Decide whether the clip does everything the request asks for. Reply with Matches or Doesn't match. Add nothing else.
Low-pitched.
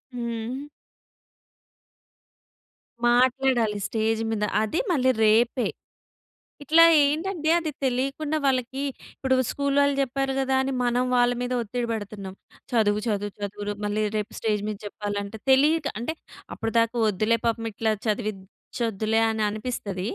Doesn't match